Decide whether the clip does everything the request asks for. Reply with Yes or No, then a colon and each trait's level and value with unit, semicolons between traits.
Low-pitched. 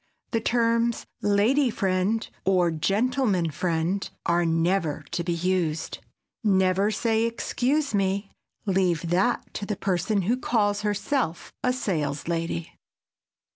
No: high, 195 Hz